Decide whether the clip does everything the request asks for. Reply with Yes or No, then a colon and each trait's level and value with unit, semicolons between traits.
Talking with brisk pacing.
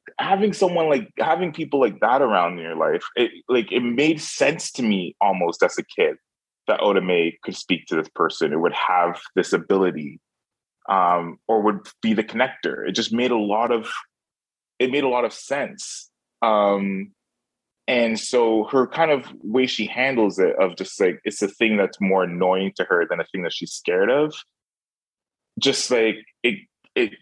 No: average, 185 wpm